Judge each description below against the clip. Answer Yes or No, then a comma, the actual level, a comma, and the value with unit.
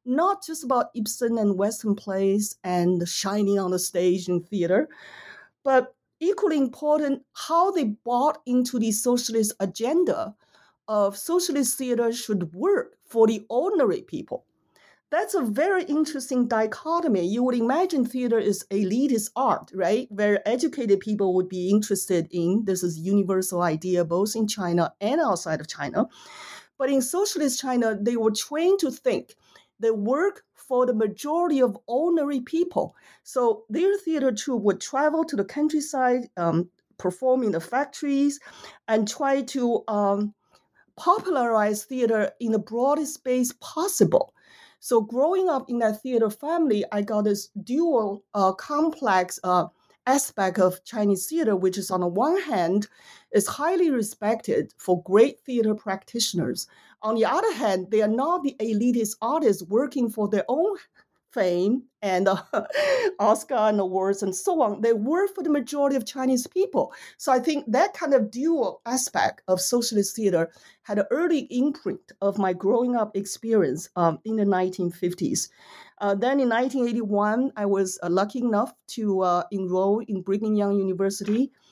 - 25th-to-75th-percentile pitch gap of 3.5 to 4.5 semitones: No, wide, 5.6 semitones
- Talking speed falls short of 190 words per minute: Yes, average, 155 wpm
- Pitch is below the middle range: No, high, 225 Hz